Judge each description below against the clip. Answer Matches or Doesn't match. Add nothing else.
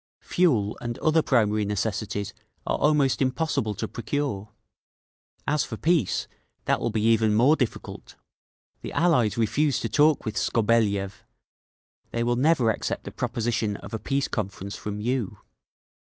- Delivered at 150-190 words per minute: Doesn't match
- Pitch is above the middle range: Doesn't match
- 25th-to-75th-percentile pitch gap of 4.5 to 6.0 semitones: Matches